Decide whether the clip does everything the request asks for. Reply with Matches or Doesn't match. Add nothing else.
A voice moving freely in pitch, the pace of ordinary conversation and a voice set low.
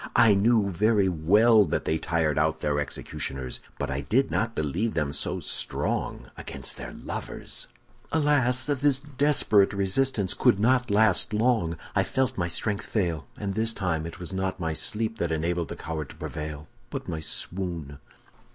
Matches